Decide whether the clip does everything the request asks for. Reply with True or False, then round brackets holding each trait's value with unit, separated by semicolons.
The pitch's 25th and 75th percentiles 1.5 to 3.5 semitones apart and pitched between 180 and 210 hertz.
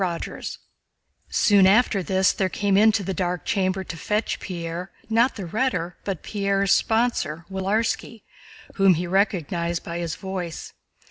True (2.9 semitones; 190 Hz)